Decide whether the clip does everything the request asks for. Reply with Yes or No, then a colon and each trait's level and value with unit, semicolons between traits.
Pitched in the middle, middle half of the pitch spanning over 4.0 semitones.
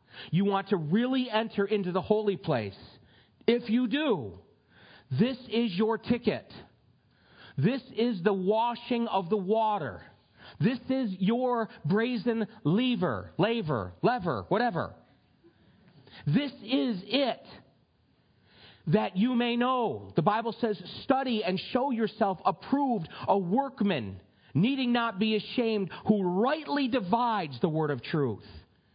No: high, 215 Hz; wide, 5.4 semitones